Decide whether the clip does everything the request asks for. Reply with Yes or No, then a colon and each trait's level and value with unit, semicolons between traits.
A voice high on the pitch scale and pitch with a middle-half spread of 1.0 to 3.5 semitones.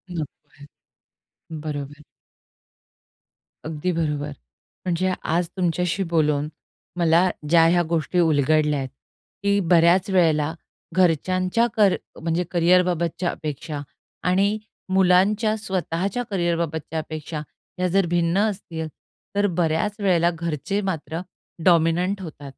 No: medium, 170 Hz; average, 2.8 semitones